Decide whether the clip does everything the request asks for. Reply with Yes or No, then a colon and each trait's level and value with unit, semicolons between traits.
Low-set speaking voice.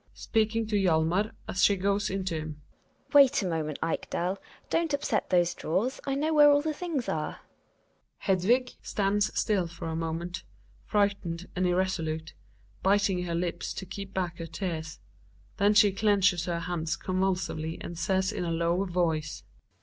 No: medium, 185 Hz